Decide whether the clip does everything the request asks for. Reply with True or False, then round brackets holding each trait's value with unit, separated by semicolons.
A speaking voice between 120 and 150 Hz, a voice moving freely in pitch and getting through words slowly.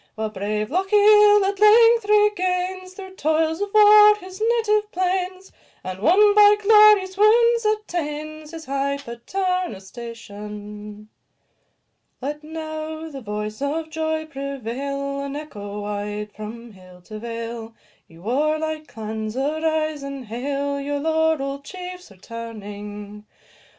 False (300 Hz; 8.5 semitones; 120 wpm)